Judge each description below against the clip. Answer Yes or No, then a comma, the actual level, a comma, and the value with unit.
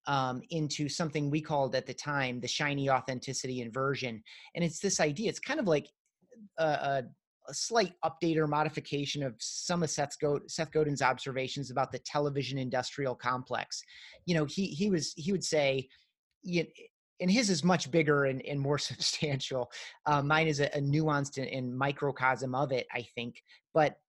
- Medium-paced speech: Yes, average, 175 wpm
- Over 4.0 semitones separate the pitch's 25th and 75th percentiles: No, average, 3.3 semitones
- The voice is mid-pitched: Yes, medium, 145 Hz